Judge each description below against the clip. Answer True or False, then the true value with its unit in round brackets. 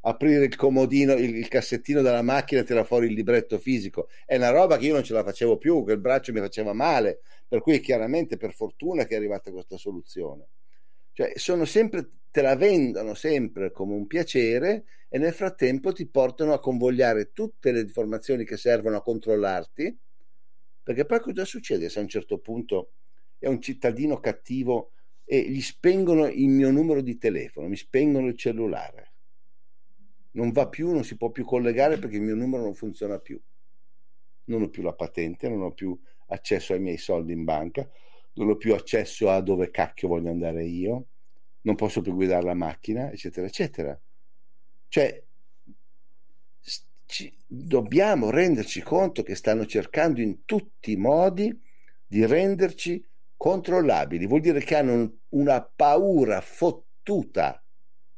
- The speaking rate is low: False (165 wpm)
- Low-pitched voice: True (125 Hz)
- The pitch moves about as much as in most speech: False (6.0 semitones)